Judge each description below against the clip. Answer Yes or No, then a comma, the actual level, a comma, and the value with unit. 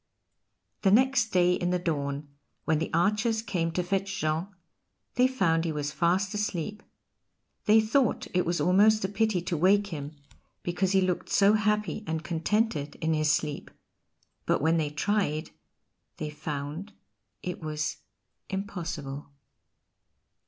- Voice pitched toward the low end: No, medium, 180 Hz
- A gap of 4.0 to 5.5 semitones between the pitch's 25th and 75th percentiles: Yes, average, 4.7 semitones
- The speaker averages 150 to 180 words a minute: No, average, 140 wpm